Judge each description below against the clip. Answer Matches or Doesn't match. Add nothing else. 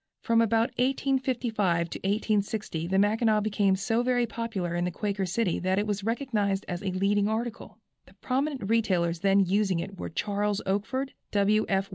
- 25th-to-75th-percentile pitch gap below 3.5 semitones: Matches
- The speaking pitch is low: Doesn't match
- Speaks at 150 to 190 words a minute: Matches